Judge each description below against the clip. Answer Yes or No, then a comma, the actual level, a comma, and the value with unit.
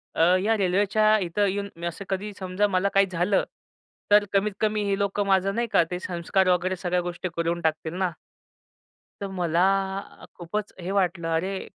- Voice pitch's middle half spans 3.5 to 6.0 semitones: No, narrow, 2.4 semitones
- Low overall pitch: No, high, 190 Hz